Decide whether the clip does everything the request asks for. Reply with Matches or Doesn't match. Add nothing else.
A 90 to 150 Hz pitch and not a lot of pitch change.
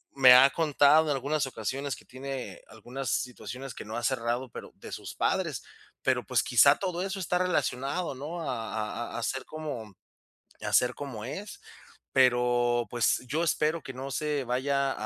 Doesn't match